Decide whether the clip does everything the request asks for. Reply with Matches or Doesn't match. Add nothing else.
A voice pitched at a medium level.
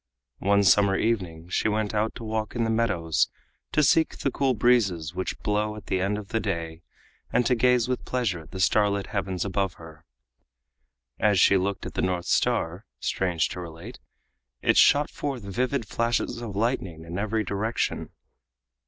Doesn't match